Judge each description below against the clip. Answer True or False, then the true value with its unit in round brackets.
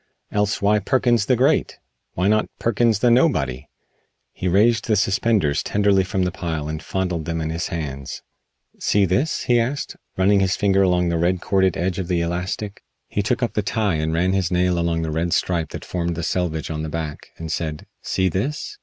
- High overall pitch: False (90 Hz)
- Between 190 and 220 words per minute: True (200 wpm)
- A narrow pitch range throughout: False (3.8 semitones)